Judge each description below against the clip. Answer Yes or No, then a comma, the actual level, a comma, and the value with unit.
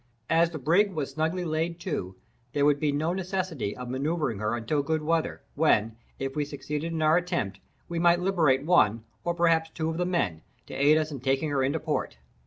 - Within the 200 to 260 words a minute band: Yes, fast, 205 wpm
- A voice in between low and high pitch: Yes, medium, 155 Hz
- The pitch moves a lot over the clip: No, average, 3.9 semitones